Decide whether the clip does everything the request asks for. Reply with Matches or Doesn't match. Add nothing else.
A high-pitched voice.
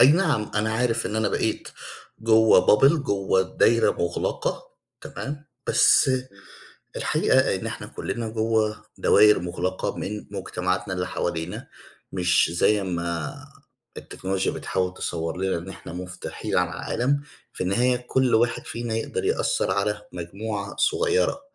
Doesn't match